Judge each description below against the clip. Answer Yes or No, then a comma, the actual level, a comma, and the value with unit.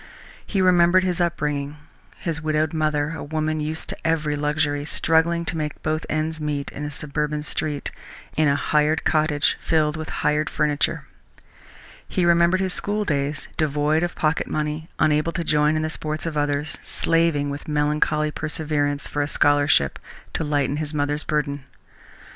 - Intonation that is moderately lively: No, narrow, 1.4 semitones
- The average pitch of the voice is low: No, medium, 150 Hz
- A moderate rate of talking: Yes, average, 160 wpm